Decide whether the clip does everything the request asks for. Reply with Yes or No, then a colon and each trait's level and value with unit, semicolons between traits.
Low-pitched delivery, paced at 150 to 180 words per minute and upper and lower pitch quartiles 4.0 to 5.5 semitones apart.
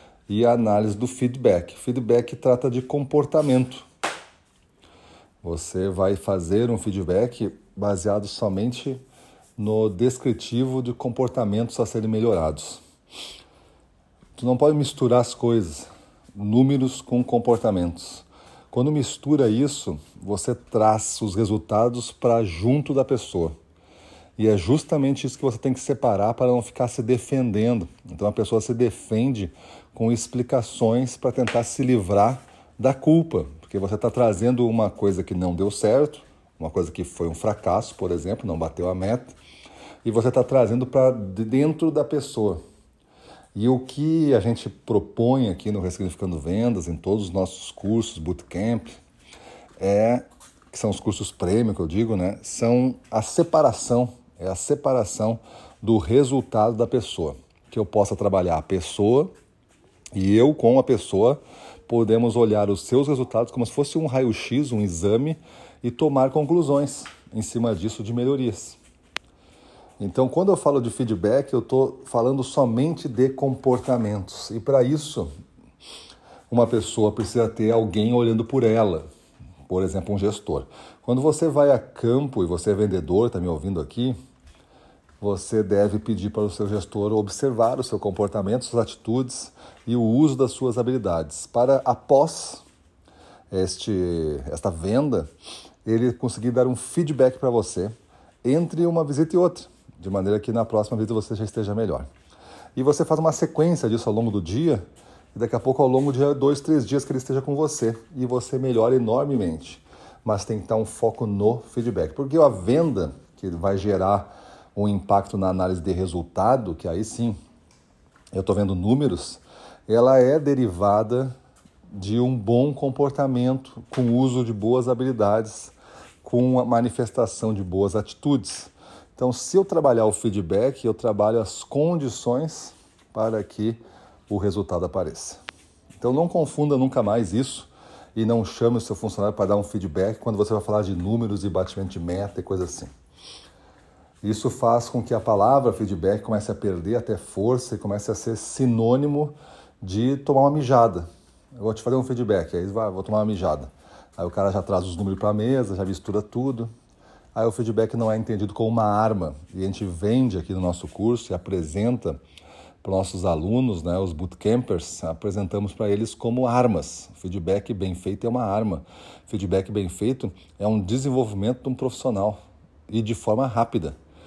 Yes: low, 115 Hz; average, 160 wpm; average, 4.3 semitones